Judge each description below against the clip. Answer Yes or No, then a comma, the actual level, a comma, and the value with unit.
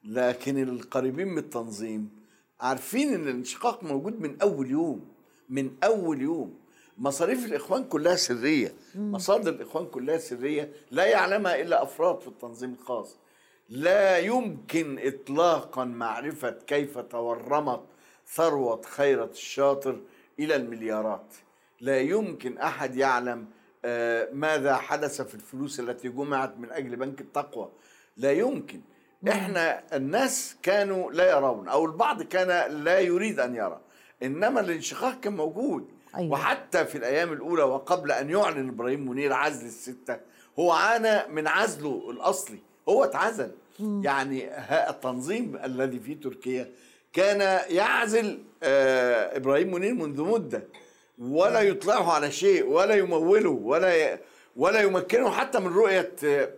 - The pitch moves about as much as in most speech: No, wide, 8.2 semitones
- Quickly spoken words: No, average, 120 wpm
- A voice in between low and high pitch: Yes, medium, 150 Hz